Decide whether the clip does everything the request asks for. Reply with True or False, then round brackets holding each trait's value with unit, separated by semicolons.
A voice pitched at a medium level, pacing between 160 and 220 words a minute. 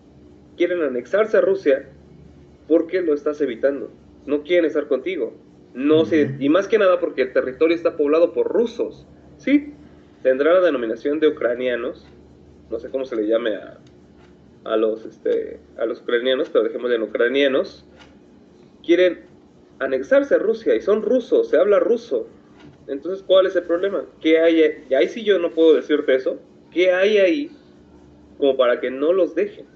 True (175 Hz; 165 wpm)